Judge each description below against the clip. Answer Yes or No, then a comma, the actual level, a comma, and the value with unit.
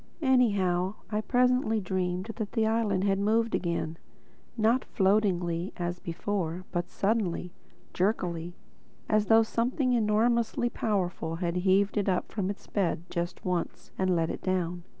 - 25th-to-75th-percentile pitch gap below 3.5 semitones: No, average, 3.8 semitones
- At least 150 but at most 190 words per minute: No, slow, 135 wpm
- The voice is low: No, high, 195 Hz